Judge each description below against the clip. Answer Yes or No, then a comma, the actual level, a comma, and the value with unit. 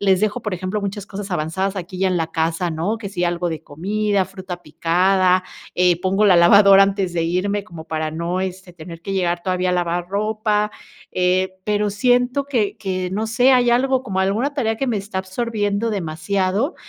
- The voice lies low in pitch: No, high, 190 Hz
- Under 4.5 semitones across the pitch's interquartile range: Yes, average, 2.9 semitones